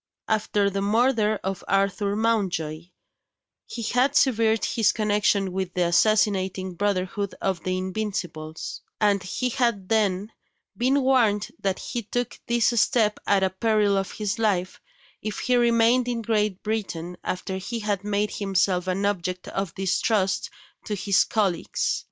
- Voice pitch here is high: Yes, high, 205 Hz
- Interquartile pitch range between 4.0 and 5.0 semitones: No, average, 2.9 semitones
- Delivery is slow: No, average, 145 wpm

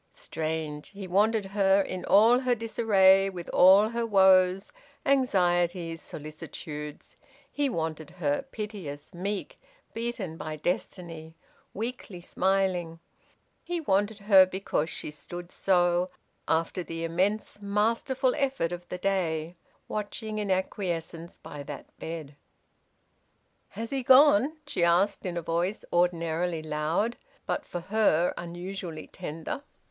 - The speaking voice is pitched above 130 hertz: Yes, medium, 185 Hz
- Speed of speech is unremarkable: No, slow, 120 wpm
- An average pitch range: Yes, average, 4.0 semitones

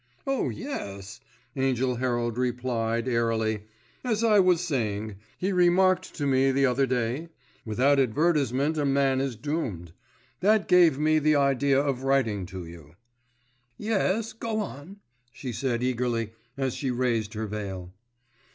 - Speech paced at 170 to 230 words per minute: No, average, 140 wpm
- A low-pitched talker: Yes, low, 130 Hz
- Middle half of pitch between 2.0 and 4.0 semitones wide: No, average, 5.3 semitones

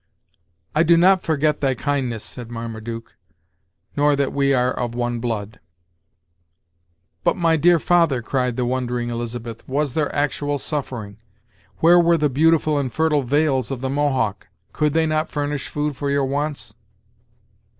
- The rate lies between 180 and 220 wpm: No, average, 150 wpm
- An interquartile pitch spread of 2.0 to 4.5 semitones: Yes, average, 3.9 semitones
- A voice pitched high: No, medium, 140 Hz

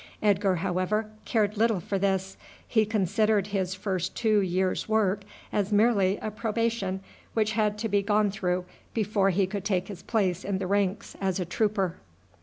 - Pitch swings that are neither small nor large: No, narrow, 2.2 semitones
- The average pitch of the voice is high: Yes, high, 200 Hz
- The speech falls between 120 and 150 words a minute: No, average, 170 wpm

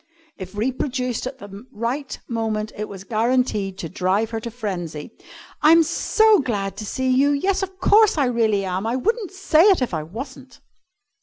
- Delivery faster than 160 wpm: Yes, average, 175 wpm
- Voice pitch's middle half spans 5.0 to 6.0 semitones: Yes, wide, 5.6 semitones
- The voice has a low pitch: No, high, 240 Hz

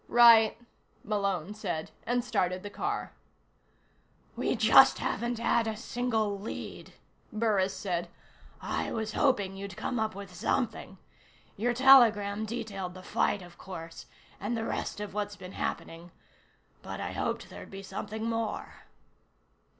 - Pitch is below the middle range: No, high, 210 Hz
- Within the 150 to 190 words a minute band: No, slow, 135 wpm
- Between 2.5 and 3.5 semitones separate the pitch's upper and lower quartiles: Yes, average, 2.9 semitones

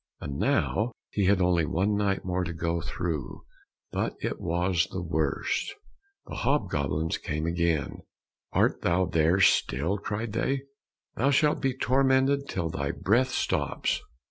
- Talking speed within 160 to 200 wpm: No, average, 145 wpm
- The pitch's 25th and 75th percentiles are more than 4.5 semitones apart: Yes, wide, 5.6 semitones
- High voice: No, very low, 90 Hz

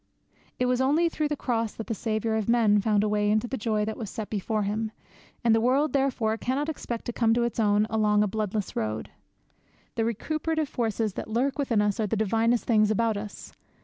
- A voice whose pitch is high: Yes, high, 225 Hz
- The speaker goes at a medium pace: No, fast, 215 wpm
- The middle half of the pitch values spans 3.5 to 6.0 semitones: No, narrow, 2.5 semitones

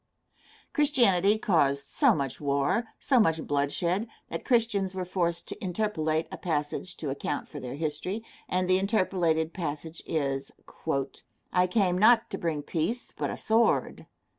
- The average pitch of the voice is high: No, medium, 175 Hz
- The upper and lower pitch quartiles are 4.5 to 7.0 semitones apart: Yes, average, 5.1 semitones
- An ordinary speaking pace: Yes, average, 145 wpm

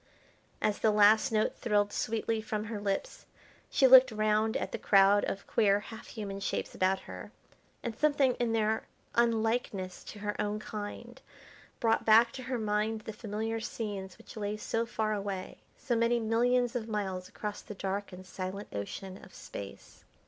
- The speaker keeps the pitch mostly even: Yes, narrow, 2.0 semitones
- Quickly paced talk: No, average, 170 wpm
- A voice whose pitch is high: Yes, high, 215 Hz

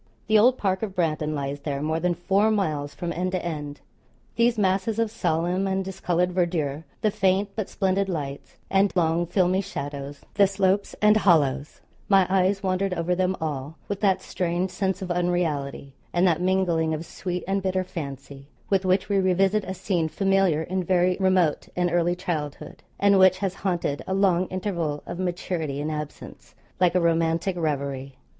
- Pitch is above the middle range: No, medium, 180 Hz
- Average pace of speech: Yes, average, 175 wpm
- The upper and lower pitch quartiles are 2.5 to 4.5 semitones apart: Yes, average, 3.2 semitones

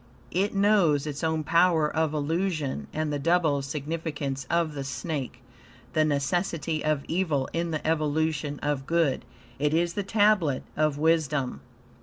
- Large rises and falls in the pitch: No, narrow, 2.6 semitones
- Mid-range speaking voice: Yes, medium, 155 Hz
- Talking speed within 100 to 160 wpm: Yes, average, 145 wpm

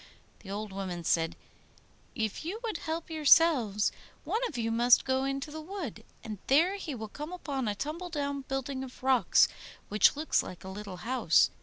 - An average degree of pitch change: No, wide, 6.8 semitones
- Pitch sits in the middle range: No, very high, 265 Hz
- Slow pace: No, average, 180 wpm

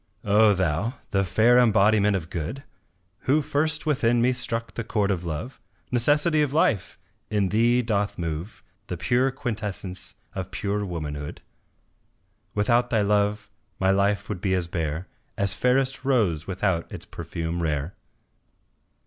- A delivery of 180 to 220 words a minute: No, average, 140 wpm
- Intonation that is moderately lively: Yes, average, 5.0 semitones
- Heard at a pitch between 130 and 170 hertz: No, low, 105 Hz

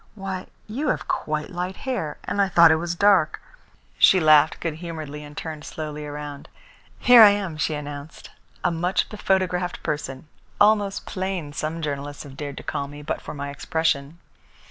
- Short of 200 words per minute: Yes, average, 170 wpm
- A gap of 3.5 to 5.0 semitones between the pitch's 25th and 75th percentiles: Yes, average, 4.2 semitones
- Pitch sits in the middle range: Yes, medium, 160 Hz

